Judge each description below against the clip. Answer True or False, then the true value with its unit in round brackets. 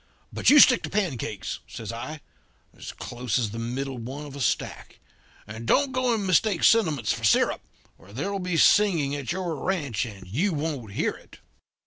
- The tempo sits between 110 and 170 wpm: False (180 wpm)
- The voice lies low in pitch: False (145 Hz)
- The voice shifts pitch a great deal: True (8.4 semitones)